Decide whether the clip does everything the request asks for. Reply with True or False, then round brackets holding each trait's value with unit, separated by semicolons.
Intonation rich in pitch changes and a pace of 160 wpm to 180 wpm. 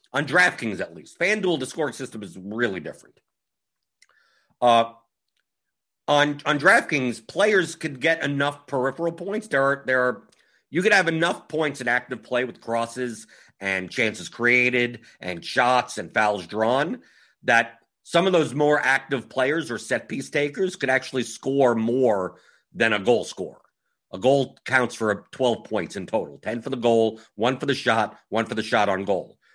False (3.9 semitones; 170 wpm)